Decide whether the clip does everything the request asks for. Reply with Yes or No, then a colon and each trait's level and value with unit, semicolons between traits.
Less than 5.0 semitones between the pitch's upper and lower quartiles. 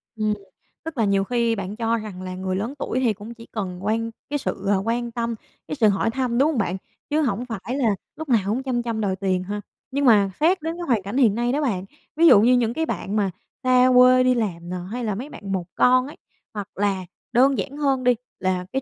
Yes: average, 4.2 semitones